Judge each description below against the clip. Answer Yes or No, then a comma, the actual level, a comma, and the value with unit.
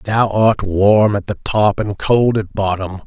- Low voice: Yes, low, 105 Hz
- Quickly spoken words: No, average, 195 wpm